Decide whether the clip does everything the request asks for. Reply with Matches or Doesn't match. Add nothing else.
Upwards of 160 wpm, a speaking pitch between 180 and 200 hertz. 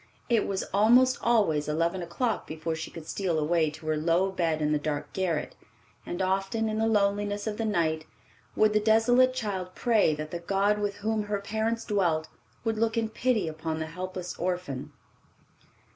Matches